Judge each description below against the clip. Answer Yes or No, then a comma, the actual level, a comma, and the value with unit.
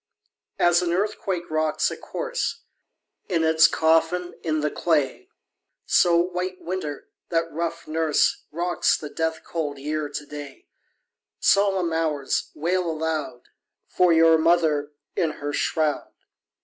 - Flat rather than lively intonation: Yes, narrow, 2.3 semitones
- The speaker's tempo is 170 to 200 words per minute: No, slow, 135 wpm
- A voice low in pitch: No, medium, 160 Hz